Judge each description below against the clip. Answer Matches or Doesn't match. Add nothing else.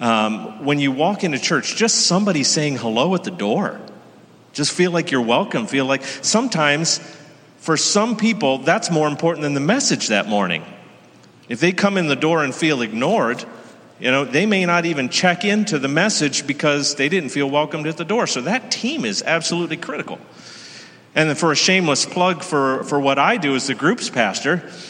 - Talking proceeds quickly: Doesn't match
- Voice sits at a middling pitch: Matches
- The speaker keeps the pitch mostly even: Doesn't match